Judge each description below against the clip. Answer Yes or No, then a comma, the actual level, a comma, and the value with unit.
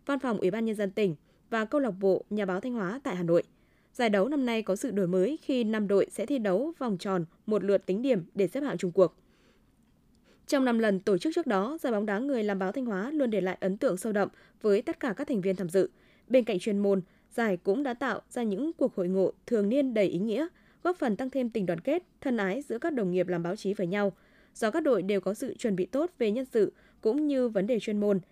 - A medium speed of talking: No, fast, 270 wpm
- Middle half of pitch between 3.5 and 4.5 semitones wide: No, wide, 5.4 semitones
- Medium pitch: No, high, 210 Hz